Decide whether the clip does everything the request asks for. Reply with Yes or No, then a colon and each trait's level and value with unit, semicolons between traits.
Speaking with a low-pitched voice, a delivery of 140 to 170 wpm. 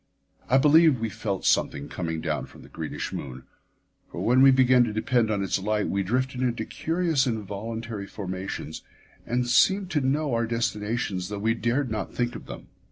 No: low, 115 Hz; average, 180 wpm